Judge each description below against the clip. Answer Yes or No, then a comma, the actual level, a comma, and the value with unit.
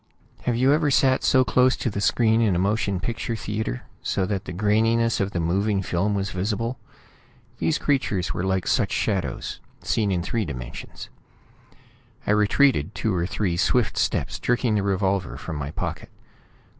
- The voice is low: Yes, low, 105 Hz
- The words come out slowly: No, average, 165 wpm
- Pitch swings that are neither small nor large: Yes, average, 3.8 semitones